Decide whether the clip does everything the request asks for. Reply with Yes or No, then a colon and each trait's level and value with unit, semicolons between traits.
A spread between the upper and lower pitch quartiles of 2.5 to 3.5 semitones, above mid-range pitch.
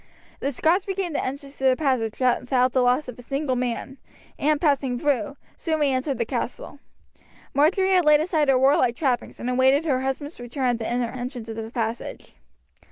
Yes: average, 3.0 semitones; very high, 265 Hz